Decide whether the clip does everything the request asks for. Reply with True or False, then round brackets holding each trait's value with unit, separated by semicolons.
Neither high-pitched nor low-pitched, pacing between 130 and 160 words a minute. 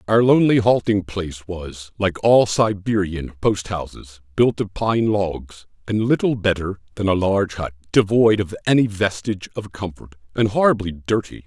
False (100 Hz; 155 wpm)